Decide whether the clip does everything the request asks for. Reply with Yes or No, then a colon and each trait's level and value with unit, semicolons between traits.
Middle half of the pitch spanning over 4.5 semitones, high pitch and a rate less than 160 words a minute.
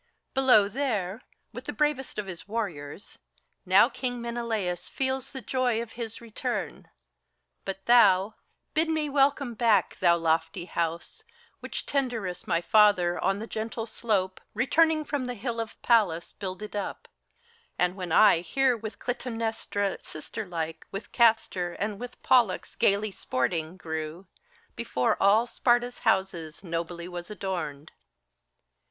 Yes: average, 5.2 semitones; high, 210 Hz; slow, 135 wpm